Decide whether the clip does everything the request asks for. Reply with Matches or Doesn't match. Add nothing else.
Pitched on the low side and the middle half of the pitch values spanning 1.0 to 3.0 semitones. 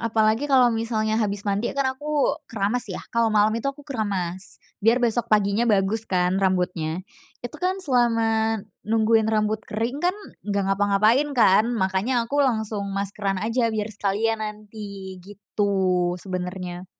Doesn't match